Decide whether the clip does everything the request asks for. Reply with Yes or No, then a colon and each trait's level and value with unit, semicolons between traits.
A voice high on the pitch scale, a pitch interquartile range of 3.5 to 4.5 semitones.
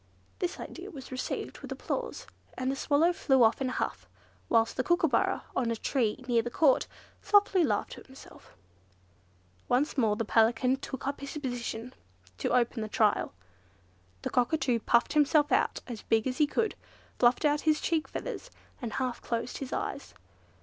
Yes: very high, 260 Hz; average, 4.1 semitones